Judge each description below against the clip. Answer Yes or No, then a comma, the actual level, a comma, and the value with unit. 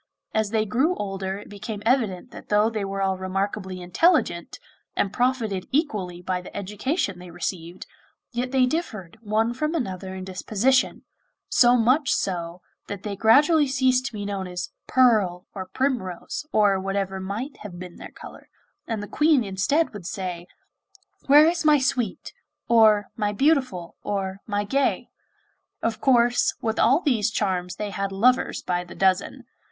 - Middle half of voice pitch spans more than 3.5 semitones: Yes, average, 5.1 semitones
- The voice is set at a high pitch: Yes, high, 205 Hz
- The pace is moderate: Yes, average, 160 wpm